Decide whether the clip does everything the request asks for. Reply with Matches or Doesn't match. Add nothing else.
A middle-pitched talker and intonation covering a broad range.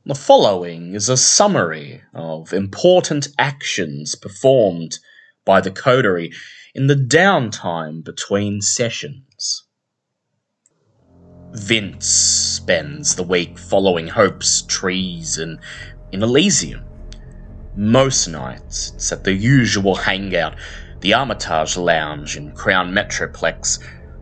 Doesn't match